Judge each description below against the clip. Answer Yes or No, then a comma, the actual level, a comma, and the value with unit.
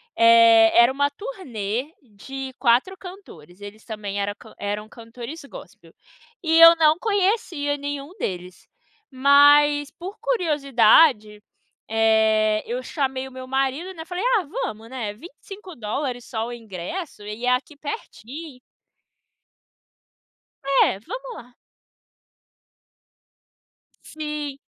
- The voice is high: Yes, very high, 265 Hz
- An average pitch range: No, wide, 6.1 semitones